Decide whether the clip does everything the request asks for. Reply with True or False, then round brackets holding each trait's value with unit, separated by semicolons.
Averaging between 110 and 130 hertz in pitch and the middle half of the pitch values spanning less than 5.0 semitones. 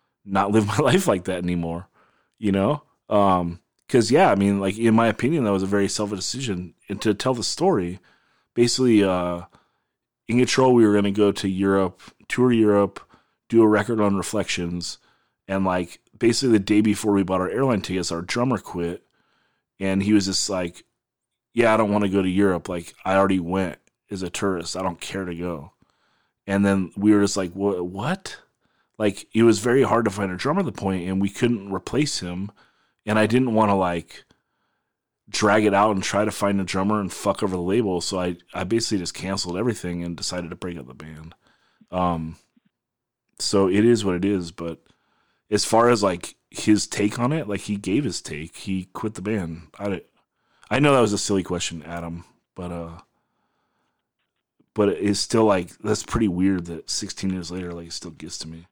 False (100 Hz; 2.9 semitones)